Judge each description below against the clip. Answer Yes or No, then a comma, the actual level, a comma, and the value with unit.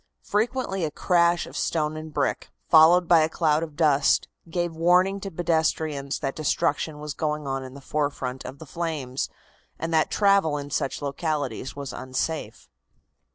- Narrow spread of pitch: No, average, 3.2 semitones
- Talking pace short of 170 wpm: Yes, average, 160 wpm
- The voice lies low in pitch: No, medium, 155 Hz